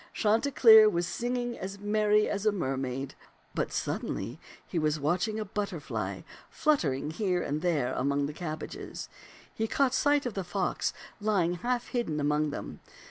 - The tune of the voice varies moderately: No, wide, 6.3 semitones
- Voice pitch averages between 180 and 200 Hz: Yes, high, 190 Hz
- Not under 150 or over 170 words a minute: Yes, average, 160 wpm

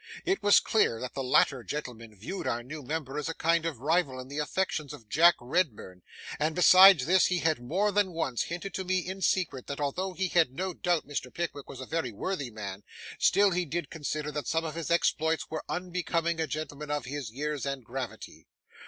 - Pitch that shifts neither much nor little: Yes, average, 4.9 semitones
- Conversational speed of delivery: No, fast, 210 wpm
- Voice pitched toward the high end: No, medium, 155 Hz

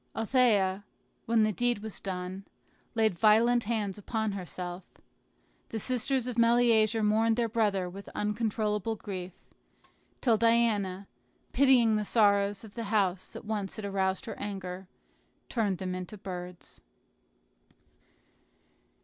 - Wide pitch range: No, average, 2.9 semitones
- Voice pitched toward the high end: Yes, high, 210 Hz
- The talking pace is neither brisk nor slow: No, slow, 125 wpm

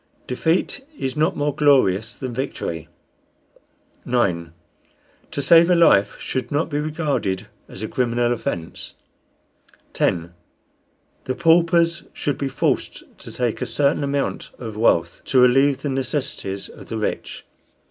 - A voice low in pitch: Yes, low, 130 Hz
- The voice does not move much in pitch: No, average, 5.0 semitones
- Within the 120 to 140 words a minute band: Yes, slow, 135 wpm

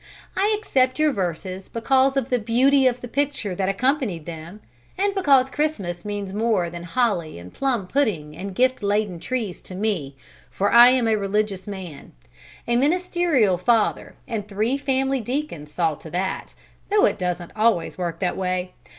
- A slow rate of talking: No, average, 170 wpm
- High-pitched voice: Yes, high, 215 Hz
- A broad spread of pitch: Yes, wide, 6.3 semitones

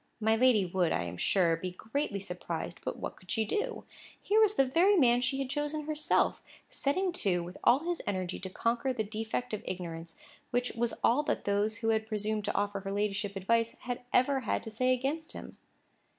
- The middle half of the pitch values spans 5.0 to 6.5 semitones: Yes, average, 5.3 semitones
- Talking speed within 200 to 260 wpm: Yes, fast, 205 wpm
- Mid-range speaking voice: No, high, 225 Hz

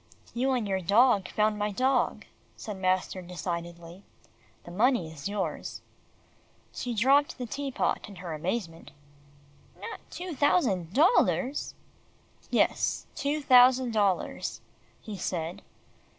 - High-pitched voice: Yes, high, 210 Hz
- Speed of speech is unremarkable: No, slow, 120 wpm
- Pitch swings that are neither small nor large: No, wide, 6.1 semitones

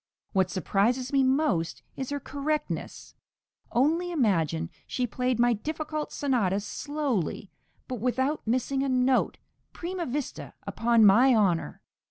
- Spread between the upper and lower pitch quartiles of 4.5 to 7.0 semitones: Yes, average, 5.1 semitones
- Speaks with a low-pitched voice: No, very high, 255 Hz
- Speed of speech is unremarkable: No, slow, 125 wpm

